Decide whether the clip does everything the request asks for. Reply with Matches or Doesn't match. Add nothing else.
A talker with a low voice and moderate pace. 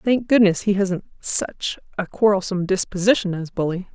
Doesn't match